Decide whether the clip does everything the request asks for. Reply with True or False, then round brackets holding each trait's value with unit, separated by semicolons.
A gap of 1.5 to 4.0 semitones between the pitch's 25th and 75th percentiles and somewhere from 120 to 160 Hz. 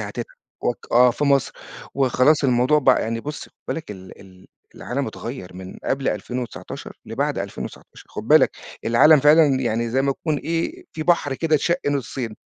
False (4.4 semitones; 135 Hz)